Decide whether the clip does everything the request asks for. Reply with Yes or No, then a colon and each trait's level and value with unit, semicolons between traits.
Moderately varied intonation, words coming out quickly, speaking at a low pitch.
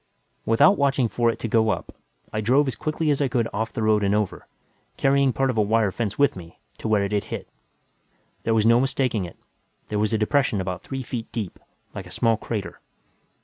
Yes: average, 3.9 semitones; fast, 220 wpm; low, 115 Hz